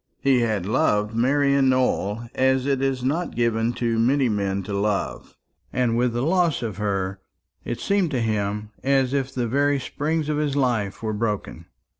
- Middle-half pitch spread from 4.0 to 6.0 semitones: Yes, average, 4.6 semitones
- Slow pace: No, average, 175 wpm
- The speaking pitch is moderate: No, low, 120 Hz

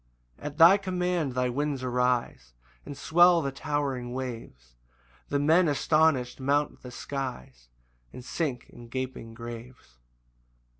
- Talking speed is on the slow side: Yes, slow, 130 wpm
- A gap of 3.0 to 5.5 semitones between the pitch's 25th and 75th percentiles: Yes, average, 3.5 semitones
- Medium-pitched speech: No, low, 130 Hz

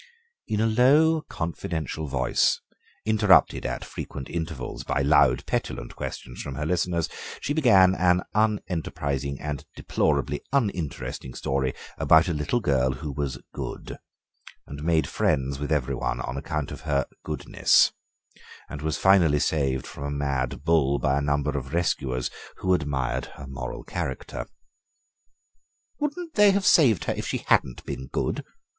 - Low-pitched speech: Yes, very low, 75 Hz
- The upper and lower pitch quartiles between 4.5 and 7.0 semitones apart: Yes, average, 5.0 semitones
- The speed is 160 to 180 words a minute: No, average, 145 wpm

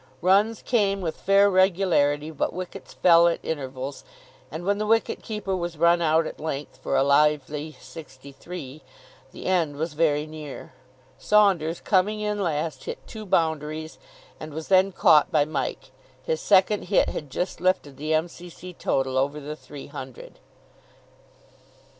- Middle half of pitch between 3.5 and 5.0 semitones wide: Yes, average, 4.1 semitones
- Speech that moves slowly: No, average, 155 wpm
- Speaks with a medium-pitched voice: Yes, medium, 160 Hz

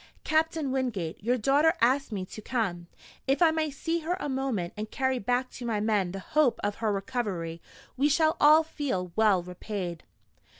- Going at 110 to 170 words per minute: No, average, 180 wpm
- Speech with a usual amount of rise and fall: No, wide, 6.7 semitones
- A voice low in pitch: No, high, 245 Hz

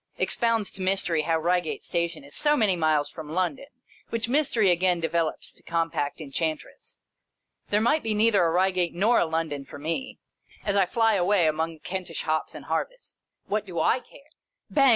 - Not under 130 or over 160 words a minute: No, average, 180 wpm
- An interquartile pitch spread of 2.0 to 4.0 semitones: No, average, 4.8 semitones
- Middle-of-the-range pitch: Yes, medium, 180 Hz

